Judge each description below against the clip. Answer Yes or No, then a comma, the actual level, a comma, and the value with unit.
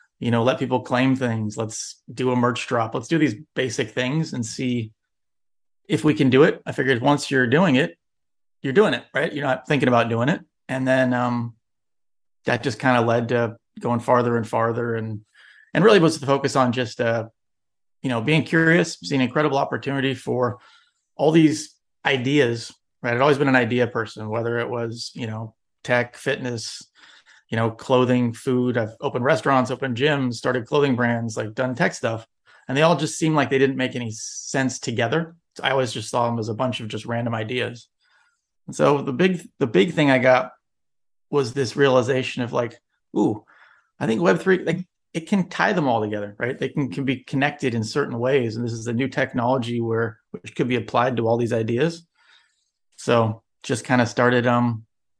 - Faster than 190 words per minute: Yes, average, 200 wpm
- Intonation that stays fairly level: No, average, 3.0 semitones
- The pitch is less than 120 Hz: No, low, 125 Hz